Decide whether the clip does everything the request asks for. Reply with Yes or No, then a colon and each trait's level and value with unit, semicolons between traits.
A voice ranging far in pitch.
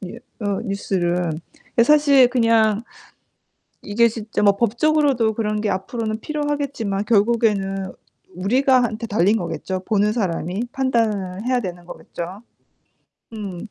No: average, 3.6 semitones